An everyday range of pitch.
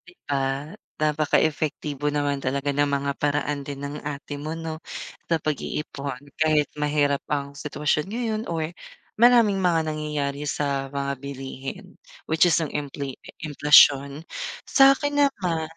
No: narrow, 2.0 semitones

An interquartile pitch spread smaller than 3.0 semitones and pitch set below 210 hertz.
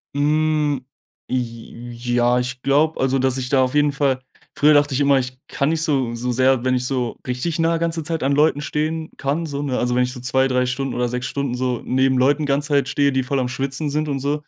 Yes: narrow, 2.6 semitones; low, 135 Hz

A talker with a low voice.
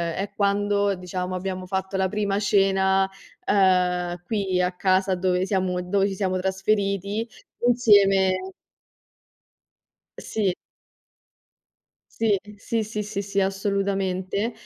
No: high, 195 Hz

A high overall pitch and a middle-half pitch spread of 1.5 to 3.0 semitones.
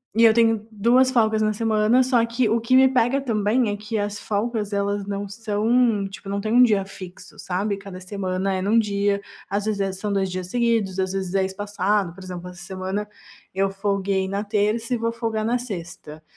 Yes: high, 205 Hz; average, 2.7 semitones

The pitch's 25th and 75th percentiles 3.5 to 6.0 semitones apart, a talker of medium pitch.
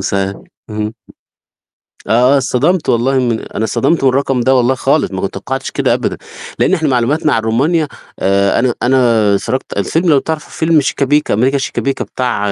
No: average, 4.2 semitones; low, 130 Hz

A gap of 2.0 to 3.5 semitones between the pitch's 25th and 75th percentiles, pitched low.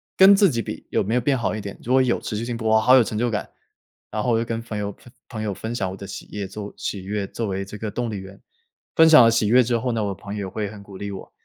Yes: average, 2.9 semitones; low, 110 Hz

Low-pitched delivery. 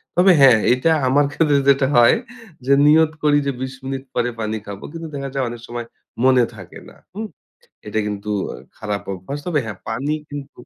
Yes: low, 130 Hz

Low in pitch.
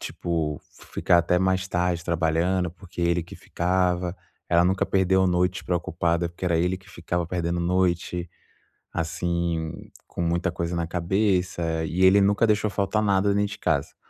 Yes: very low, 90 Hz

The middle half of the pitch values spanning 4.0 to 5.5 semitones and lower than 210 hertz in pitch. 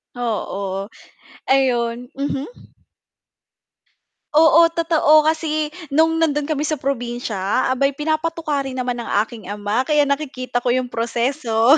No: average, 4.3 semitones; very high, 270 Hz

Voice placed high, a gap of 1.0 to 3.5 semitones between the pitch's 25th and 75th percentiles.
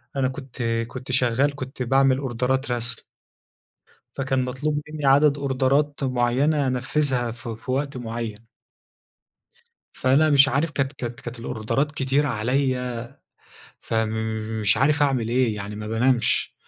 No: low, 130 Hz; average, 2.7 semitones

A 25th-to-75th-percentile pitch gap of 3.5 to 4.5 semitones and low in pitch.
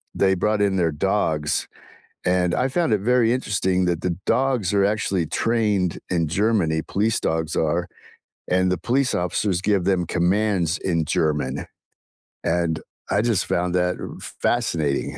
Yes: average, 3.8 semitones; very low, 90 Hz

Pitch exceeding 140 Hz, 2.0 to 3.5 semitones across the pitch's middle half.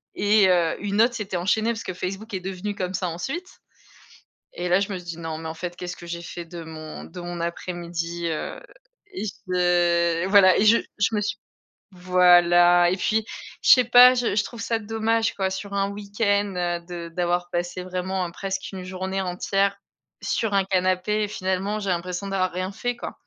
Yes: medium, 185 Hz; narrow, 2.6 semitones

